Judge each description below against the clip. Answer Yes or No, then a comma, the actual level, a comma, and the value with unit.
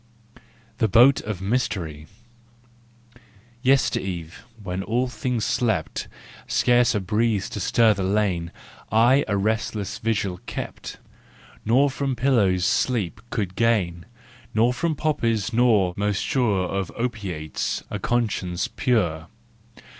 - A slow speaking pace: Yes, slow, 110 wpm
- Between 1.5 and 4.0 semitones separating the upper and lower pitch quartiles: No, average, 4.5 semitones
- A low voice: Yes, low, 110 Hz